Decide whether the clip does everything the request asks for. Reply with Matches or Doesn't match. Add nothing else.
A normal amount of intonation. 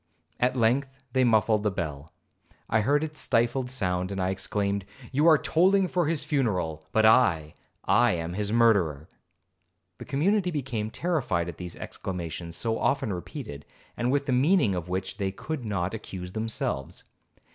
Doesn't match